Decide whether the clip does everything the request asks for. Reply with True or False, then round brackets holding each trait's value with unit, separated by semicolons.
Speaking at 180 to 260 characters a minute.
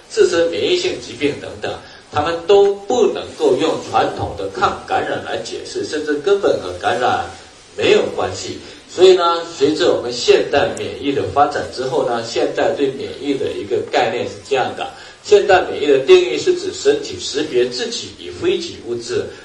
False (270 characters per minute)